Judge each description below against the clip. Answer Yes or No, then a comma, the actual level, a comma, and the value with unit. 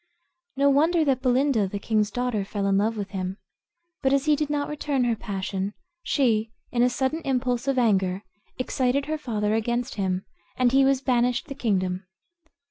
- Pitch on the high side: Yes, high, 245 Hz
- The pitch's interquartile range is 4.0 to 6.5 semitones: Yes, average, 4.8 semitones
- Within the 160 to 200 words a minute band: Yes, average, 180 wpm